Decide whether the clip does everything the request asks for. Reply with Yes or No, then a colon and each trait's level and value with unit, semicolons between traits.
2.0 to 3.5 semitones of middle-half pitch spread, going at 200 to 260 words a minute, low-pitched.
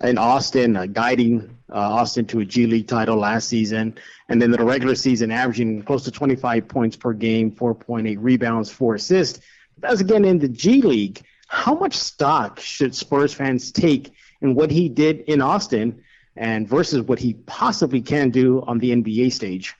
No: average, 2.9 semitones; average, 185 wpm; low, 120 Hz